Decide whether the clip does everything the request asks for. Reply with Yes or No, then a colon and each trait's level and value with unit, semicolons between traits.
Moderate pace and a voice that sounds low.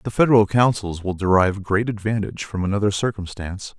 Yes: average, 160 wpm; low, 100 Hz